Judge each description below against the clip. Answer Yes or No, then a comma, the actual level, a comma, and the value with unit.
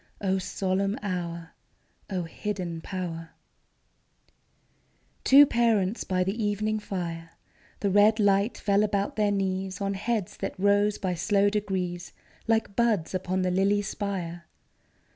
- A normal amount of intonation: No, narrow, 2.1 semitones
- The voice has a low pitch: No, high, 195 Hz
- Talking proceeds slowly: Yes, slow, 125 wpm